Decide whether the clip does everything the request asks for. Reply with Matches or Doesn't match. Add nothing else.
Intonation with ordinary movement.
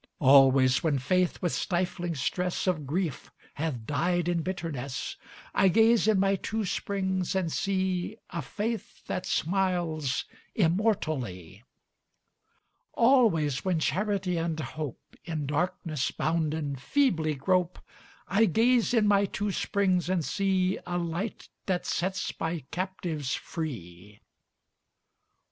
Matches